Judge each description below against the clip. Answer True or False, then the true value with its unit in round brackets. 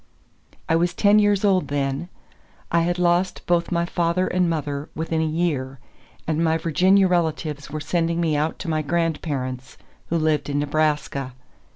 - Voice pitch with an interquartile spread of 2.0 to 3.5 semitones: True (2.8 semitones)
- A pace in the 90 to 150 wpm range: False (165 wpm)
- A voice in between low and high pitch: True (165 Hz)